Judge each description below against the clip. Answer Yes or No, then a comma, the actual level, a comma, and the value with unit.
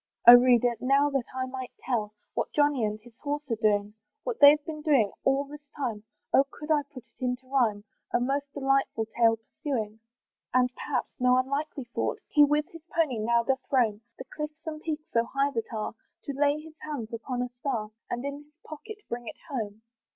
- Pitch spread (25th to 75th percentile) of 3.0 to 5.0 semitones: Yes, average, 3.8 semitones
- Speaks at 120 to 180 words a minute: No, average, 200 wpm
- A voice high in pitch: Yes, very high, 260 Hz